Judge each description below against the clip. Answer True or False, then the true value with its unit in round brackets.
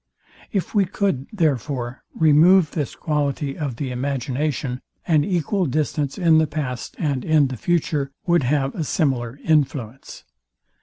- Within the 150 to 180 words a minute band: False (140 wpm)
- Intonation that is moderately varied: True (3.2 semitones)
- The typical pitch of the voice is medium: True (145 Hz)